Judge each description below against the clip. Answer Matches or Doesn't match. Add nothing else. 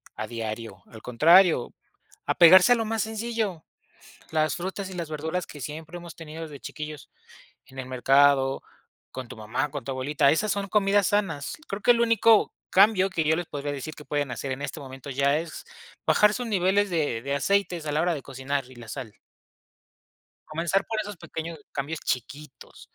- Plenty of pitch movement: Matches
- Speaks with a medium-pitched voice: Matches